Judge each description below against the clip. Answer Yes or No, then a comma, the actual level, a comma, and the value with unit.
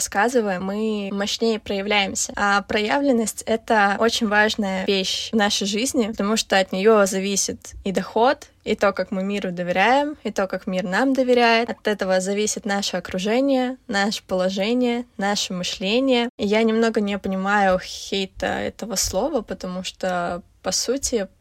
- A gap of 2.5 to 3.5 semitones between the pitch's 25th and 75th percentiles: Yes, average, 2.9 semitones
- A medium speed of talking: Yes, average, 150 wpm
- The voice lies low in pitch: No, high, 205 Hz